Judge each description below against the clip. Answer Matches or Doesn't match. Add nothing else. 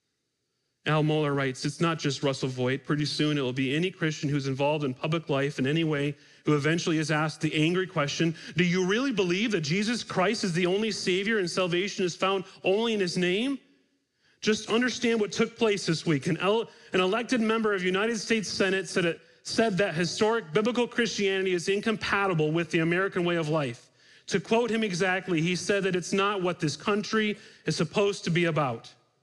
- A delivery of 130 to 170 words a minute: Doesn't match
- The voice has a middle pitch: Matches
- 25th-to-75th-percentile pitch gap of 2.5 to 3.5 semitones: Doesn't match